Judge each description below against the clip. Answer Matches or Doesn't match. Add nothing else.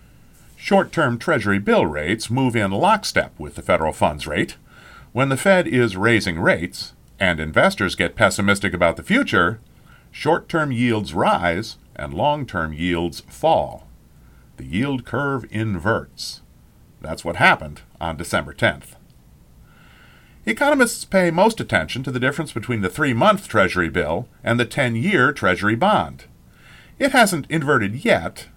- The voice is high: Doesn't match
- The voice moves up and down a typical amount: Doesn't match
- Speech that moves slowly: Doesn't match